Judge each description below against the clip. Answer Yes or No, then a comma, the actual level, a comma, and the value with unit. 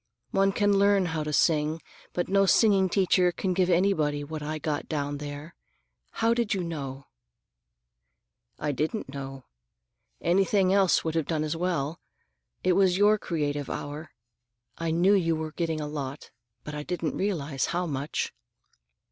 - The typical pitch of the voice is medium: Yes, medium, 165 Hz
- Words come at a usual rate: Yes, average, 155 wpm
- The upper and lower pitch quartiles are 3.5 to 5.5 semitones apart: Yes, average, 4.2 semitones